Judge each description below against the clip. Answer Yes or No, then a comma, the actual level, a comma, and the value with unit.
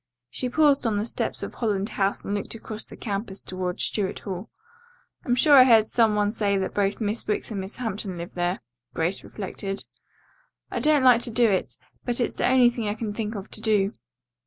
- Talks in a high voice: Yes, high, 210 Hz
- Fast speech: Yes, fast, 210 wpm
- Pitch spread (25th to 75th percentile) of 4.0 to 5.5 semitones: No, average, 3.2 semitones